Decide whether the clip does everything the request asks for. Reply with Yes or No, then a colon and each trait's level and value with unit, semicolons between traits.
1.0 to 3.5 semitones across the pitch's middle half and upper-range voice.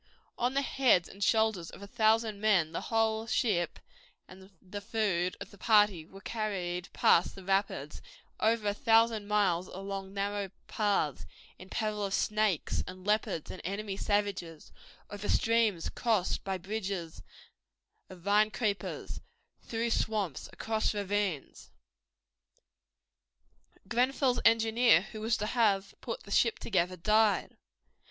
Yes: average, 2.7 semitones; high, 205 Hz